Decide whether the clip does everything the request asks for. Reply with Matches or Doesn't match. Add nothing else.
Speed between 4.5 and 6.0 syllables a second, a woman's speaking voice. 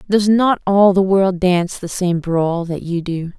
Doesn't match